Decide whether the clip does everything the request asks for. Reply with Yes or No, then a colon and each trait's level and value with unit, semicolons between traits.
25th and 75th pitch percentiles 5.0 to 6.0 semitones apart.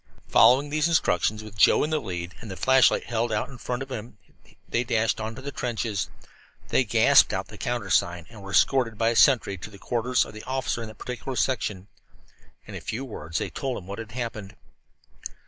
No: average, 3.8 semitones